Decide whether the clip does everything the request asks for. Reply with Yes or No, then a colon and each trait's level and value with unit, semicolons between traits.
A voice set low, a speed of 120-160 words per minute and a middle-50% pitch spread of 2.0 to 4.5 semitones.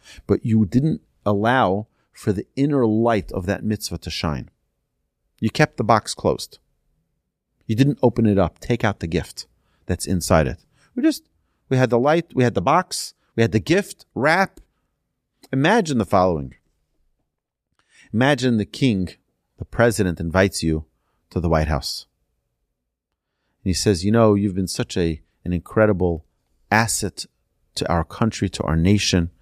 No: low, 100 Hz; average, 155 wpm; wide, 5.5 semitones